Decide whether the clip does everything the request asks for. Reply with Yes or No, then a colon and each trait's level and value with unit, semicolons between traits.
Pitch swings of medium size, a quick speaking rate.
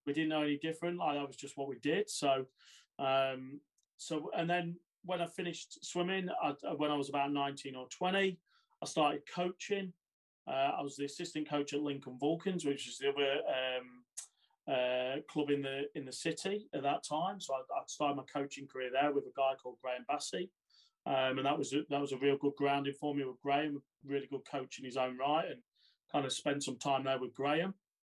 Yes: average, 3.2 semitones; fast, 215 wpm